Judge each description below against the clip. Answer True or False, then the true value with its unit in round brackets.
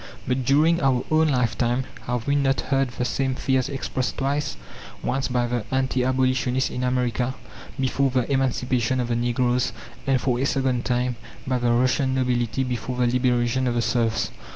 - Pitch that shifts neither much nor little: False (1.4 semitones)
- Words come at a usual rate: True (175 wpm)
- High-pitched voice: False (125 Hz)